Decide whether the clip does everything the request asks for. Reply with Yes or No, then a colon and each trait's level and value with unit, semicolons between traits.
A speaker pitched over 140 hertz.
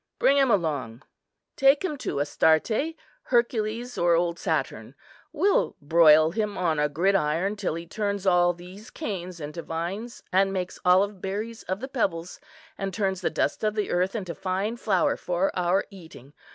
Yes: high, 190 Hz